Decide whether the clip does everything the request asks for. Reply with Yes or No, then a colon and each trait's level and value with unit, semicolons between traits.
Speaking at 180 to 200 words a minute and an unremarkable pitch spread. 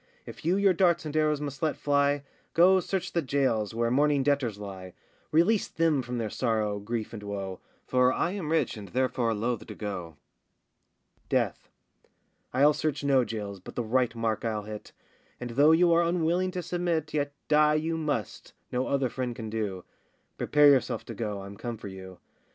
No: average, 185 wpm; wide, 6.0 semitones